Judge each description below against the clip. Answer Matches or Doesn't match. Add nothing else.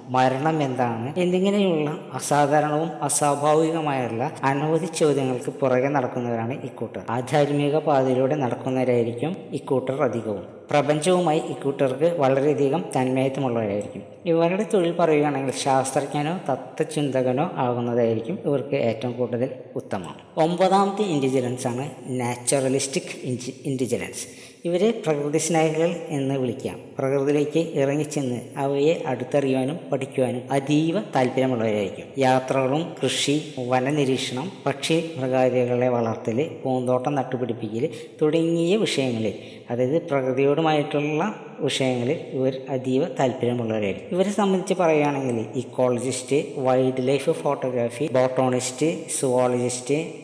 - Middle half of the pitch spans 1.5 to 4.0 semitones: Matches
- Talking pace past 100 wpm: Doesn't match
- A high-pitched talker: Doesn't match